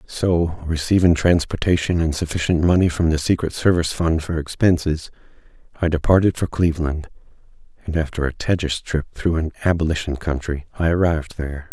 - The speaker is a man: Yes, male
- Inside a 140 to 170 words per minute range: Yes, average, 150 wpm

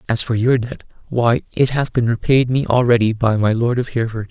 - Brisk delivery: Yes, fast, 225 wpm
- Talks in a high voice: No, low, 120 Hz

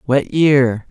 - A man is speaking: Yes, male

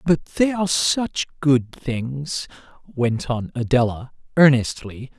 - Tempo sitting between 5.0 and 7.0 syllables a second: No, 3.6 syllables/s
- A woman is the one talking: No, male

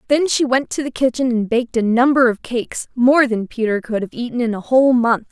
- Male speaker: No, female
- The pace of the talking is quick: Yes, fast, 250 wpm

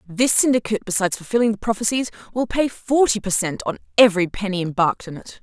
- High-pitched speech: Yes, high, 210 Hz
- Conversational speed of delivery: Yes, average, 190 wpm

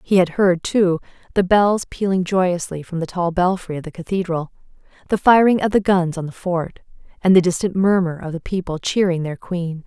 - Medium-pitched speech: Yes, medium, 180 Hz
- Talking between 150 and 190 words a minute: No, average, 200 wpm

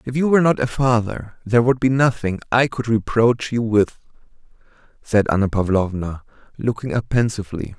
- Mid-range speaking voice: No, low, 115 Hz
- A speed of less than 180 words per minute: Yes, average, 160 wpm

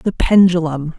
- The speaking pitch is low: No, medium, 170 Hz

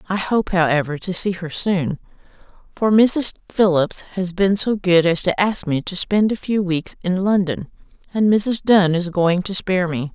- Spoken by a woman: Yes, female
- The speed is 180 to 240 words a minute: Yes, average, 195 wpm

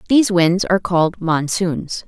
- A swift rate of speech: No, average, 145 wpm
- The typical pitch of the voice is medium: Yes, medium, 180 Hz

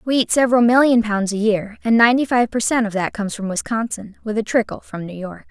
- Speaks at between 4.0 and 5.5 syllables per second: No, 6.1 syllables/s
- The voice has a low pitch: No, high, 220 Hz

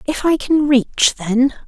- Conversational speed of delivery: Yes, average, 180 wpm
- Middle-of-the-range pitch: No, very high, 270 Hz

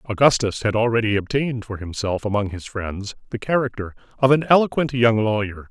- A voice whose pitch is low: Yes, low, 115 Hz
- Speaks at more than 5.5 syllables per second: Yes, 5.7 syllables/s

